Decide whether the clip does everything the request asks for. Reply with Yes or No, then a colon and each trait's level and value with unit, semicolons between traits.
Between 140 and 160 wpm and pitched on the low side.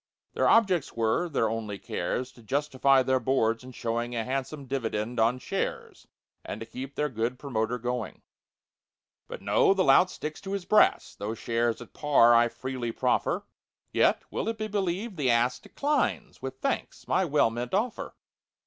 Yes: average, 155 wpm; low, 130 Hz